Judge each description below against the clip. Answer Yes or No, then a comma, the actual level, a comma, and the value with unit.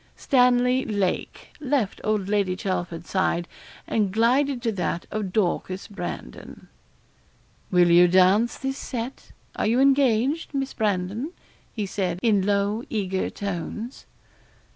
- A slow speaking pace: Yes, slow, 120 wpm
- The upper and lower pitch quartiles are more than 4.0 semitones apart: Yes, average, 4.8 semitones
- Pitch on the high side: Yes, high, 210 Hz